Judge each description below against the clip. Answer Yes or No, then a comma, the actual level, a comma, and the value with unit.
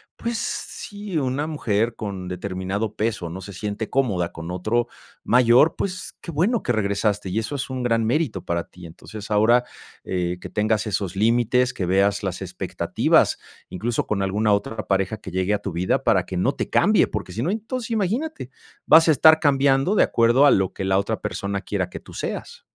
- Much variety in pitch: Yes, wide, 5.9 semitones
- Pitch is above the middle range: No, low, 110 Hz